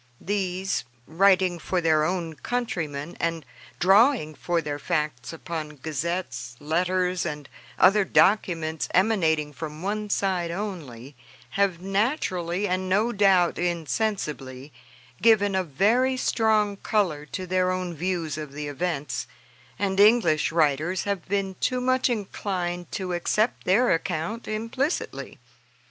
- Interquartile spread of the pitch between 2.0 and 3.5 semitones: No, average, 4.2 semitones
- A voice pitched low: No, medium, 180 Hz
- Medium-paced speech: No, slow, 125 wpm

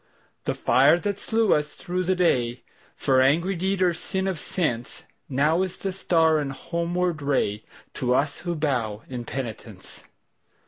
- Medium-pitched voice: Yes, medium, 155 Hz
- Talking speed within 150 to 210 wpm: No, average, 140 wpm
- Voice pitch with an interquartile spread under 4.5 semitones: No, wide, 5.5 semitones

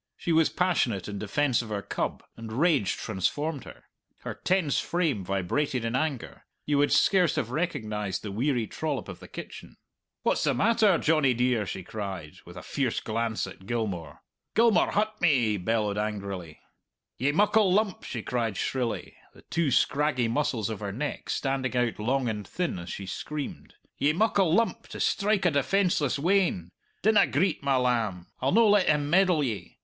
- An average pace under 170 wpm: No, average, 175 wpm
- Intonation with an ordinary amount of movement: No, wide, 7.7 semitones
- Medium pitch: No, low, 130 Hz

